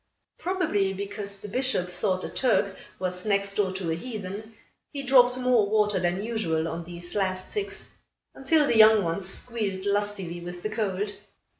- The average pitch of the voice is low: No, high, 200 Hz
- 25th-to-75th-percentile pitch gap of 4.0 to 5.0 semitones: No, average, 3.1 semitones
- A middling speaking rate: Yes, average, 165 wpm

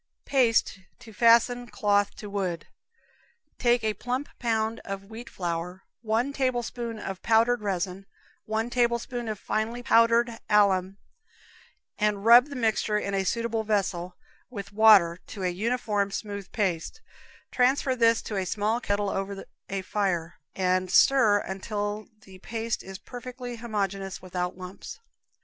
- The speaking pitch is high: Yes, high, 215 Hz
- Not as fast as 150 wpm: Yes, slow, 135 wpm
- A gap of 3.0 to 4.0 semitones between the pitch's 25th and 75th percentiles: Yes, average, 3.3 semitones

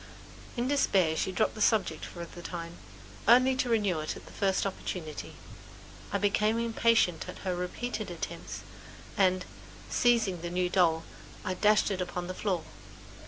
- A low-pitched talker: No, medium, 185 Hz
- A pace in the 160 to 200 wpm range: Yes, average, 165 wpm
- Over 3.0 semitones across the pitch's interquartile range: Yes, average, 3.8 semitones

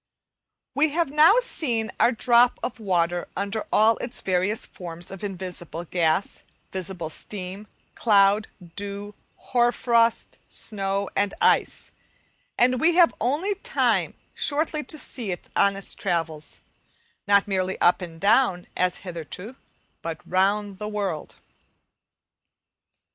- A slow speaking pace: Yes, slow, 125 wpm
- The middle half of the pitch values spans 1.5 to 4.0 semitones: No, average, 4.7 semitones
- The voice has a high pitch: Yes, high, 200 Hz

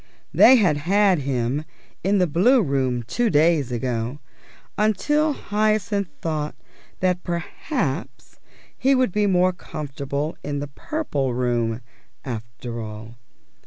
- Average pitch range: No, wide, 8.1 semitones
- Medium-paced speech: No, slow, 120 wpm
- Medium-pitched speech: Yes, medium, 155 Hz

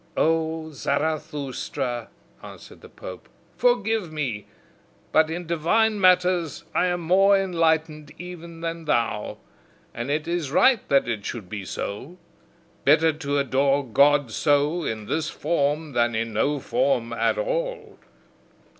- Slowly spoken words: Yes, slow, 130 wpm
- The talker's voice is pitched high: No, medium, 155 Hz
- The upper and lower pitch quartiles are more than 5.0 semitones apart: No, average, 4.1 semitones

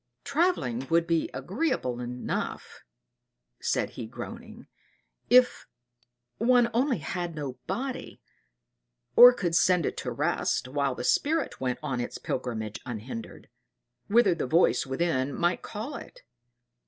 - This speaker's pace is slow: Yes, slow, 125 wpm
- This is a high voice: No, medium, 170 Hz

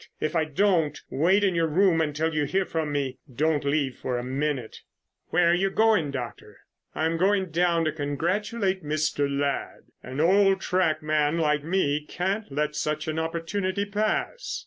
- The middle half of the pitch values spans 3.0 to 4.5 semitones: Yes, average, 4.1 semitones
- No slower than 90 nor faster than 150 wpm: No, average, 170 wpm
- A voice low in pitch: No, medium, 160 Hz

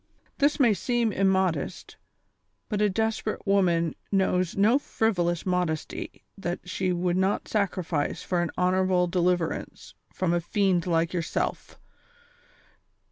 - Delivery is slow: Yes, slow, 120 wpm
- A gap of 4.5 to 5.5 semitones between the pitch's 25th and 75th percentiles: No, narrow, 2.5 semitones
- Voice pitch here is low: No, medium, 185 Hz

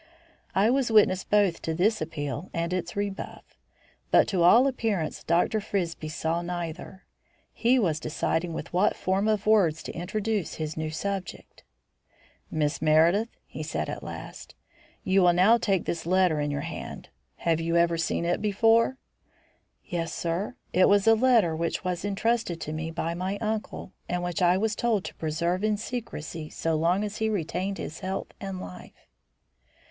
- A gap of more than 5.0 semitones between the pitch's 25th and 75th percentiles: No, average, 4.1 semitones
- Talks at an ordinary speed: Yes, average, 170 wpm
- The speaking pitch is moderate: Yes, medium, 180 Hz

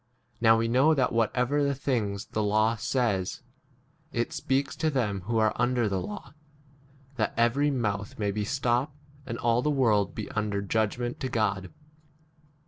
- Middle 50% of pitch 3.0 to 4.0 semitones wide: Yes, average, 3.5 semitones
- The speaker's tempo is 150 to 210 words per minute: Yes, average, 170 wpm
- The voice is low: Yes, low, 115 Hz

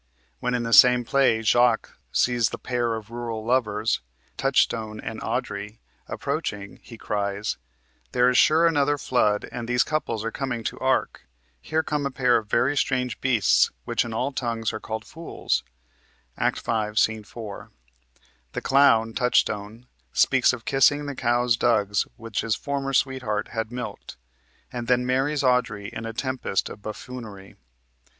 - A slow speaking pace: No, average, 155 wpm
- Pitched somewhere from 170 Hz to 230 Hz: No, low, 120 Hz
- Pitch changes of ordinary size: Yes, average, 3.0 semitones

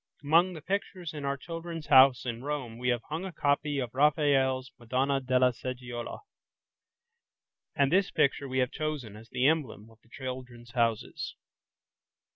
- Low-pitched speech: Yes, low, 130 Hz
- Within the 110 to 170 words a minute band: Yes, average, 155 wpm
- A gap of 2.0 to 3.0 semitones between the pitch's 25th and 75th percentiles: No, average, 3.4 semitones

